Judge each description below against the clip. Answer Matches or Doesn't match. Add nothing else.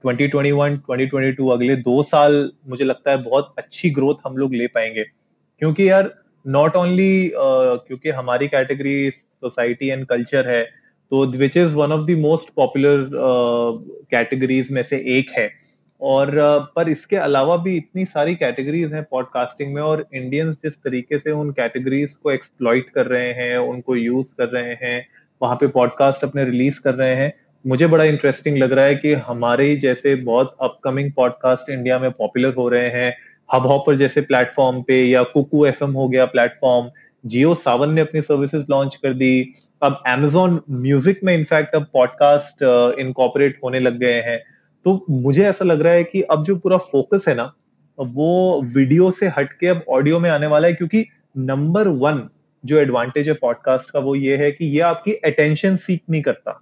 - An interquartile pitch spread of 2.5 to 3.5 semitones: Matches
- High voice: Doesn't match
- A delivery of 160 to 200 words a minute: Matches